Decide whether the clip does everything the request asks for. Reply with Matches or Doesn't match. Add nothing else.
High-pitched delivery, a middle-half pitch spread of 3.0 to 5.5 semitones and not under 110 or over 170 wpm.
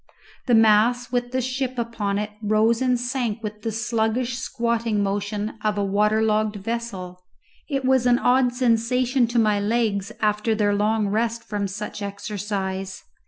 Doesn't match